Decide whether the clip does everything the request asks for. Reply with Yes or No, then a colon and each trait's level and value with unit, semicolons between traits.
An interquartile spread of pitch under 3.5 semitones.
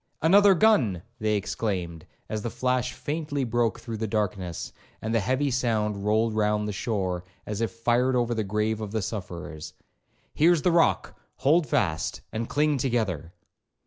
No: average, 3.8 semitones